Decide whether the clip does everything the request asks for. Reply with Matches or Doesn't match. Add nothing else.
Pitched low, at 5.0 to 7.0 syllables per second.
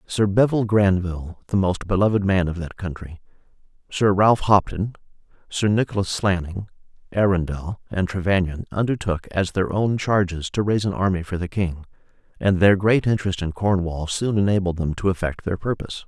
Matches